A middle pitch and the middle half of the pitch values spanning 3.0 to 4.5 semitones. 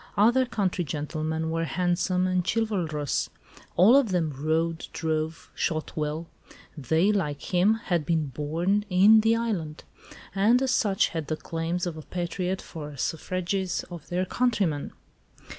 Yes: medium, 175 Hz; average, 3.8 semitones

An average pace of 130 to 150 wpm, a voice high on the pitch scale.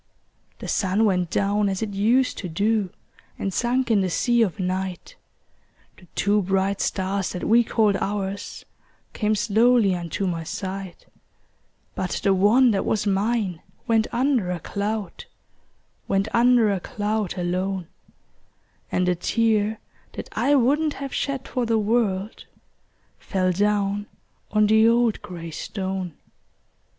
Yes: average, 140 wpm; high, 205 Hz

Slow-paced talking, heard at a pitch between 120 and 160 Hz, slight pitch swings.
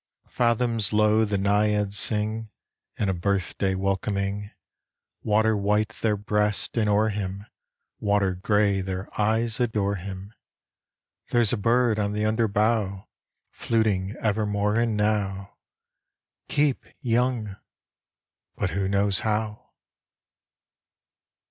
No: slow, 110 wpm; low, 105 Hz; narrow, 1.8 semitones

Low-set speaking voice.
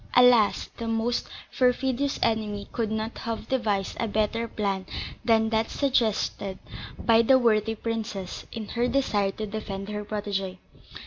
No: high, 220 Hz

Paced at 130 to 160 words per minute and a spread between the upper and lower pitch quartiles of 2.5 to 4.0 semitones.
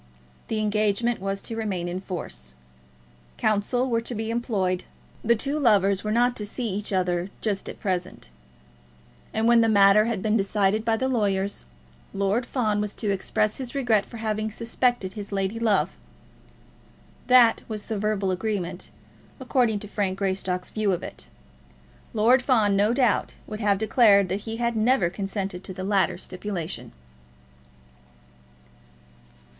Yes: average, 150 wpm; average, 2.8 semitones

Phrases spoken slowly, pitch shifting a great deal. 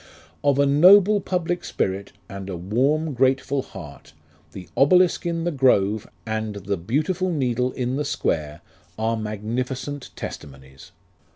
Yes: slow, 130 wpm; wide, 6.8 semitones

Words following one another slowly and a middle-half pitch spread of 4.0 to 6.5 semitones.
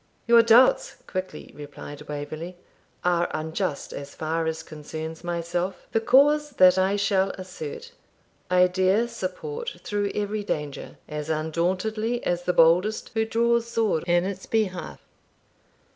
Yes: slow, 130 wpm; average, 5.2 semitones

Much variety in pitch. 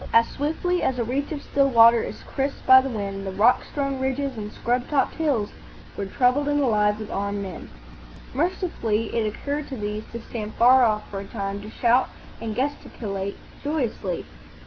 No: average, 4.8 semitones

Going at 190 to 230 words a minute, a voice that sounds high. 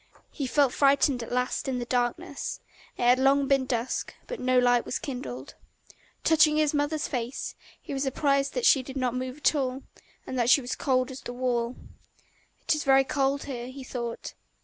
Yes: average, 195 wpm; very high, 260 Hz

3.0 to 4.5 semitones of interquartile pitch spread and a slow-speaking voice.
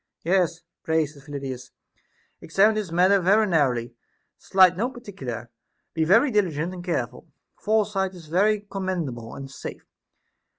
No: wide, 5.5 semitones; slow, 130 wpm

